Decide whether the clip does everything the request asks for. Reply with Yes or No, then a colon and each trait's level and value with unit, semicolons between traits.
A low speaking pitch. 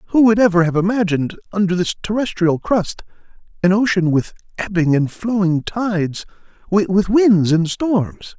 No: high, 190 Hz